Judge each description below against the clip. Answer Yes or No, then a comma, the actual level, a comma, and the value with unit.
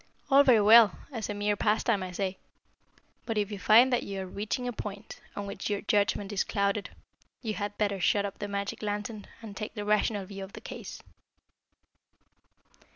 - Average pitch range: No, narrow, 1.4 semitones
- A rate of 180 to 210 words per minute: Yes, average, 190 wpm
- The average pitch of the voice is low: No, high, 205 Hz